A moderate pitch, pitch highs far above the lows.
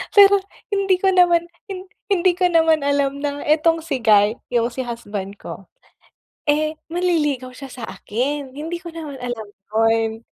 No: very high, 290 Hz; wide, 6.0 semitones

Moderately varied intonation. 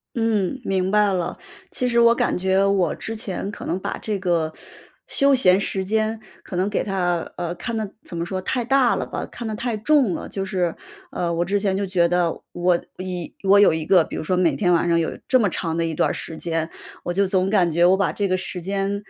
Yes: average, 3.0 semitones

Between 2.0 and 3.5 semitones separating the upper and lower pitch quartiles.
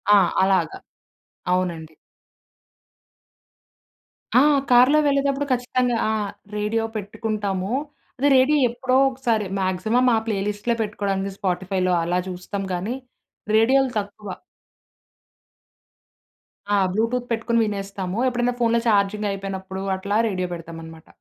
No: average, 4.1 semitones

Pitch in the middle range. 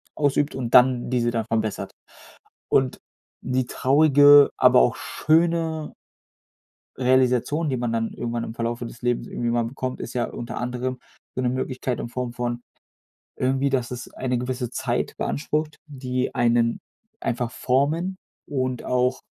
No: low, 125 Hz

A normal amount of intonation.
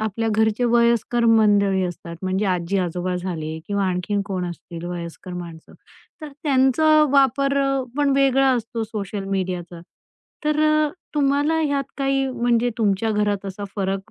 No: wide, 6.2 semitones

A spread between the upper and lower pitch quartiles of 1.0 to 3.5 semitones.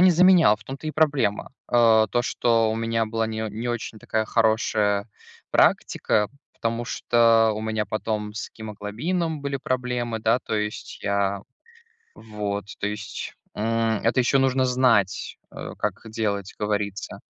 Yes: narrow, 2.4 semitones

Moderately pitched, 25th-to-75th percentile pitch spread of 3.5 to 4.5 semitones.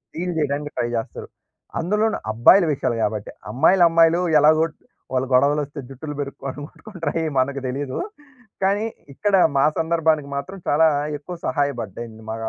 Yes: medium, 145 Hz; average, 3.8 semitones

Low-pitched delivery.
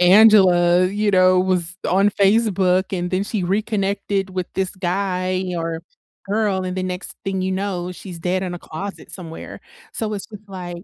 No: medium, 185 Hz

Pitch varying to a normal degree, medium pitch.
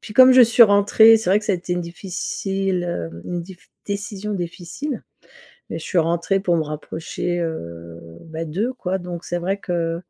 Yes: average, 3.3 semitones; medium, 180 Hz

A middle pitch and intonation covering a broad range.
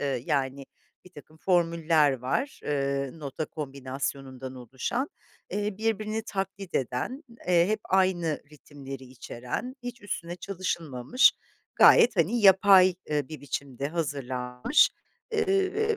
Yes: medium, 160 Hz; wide, 6.6 semitones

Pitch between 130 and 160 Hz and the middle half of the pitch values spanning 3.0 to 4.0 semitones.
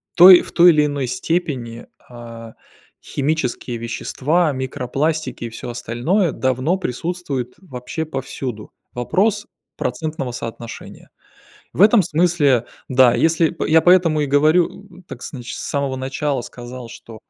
No: medium, 140 Hz; average, 5.1 semitones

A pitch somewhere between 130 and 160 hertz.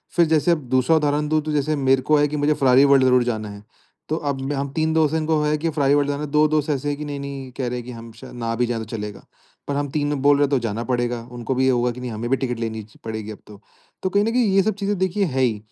Yes: medium, 140 Hz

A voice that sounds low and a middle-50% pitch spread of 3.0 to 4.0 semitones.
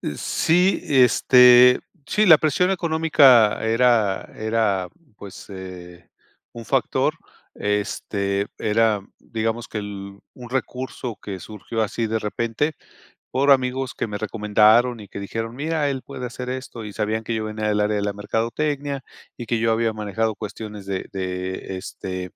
Yes: low, 110 Hz; average, 3.5 semitones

